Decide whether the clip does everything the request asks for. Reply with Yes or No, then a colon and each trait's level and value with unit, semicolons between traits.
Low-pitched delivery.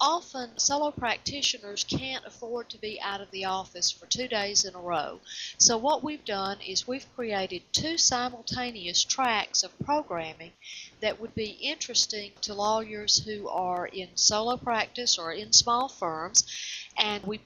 No: high, 210 Hz